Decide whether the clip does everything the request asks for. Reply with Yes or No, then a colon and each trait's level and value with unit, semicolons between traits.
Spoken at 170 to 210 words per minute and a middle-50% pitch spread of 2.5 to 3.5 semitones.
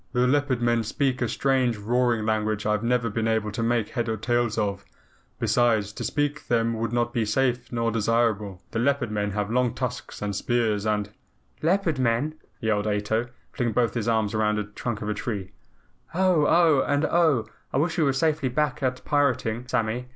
Yes: average, 195 wpm; average, 3.2 semitones